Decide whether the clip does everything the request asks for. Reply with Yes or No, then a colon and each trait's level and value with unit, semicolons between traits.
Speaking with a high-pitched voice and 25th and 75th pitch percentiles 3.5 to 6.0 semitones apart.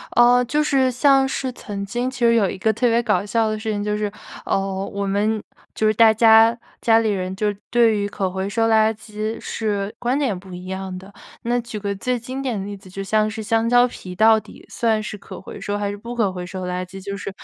No: high, 215 Hz; average, 2.8 semitones